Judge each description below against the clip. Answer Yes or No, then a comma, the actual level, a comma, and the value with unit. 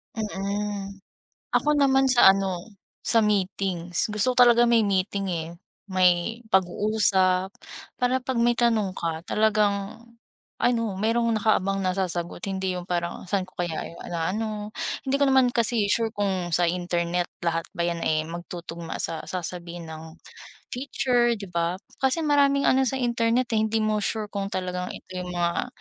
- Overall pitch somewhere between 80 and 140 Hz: No, high, 195 Hz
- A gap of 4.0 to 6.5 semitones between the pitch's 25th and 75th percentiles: Yes, average, 4.4 semitones